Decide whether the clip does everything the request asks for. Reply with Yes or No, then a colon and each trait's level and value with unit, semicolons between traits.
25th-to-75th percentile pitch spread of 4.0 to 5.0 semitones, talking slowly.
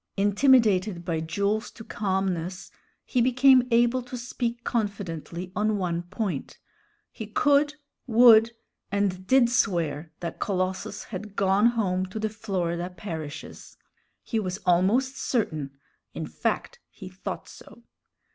Yes: average, 4.5 semitones; slow, 125 wpm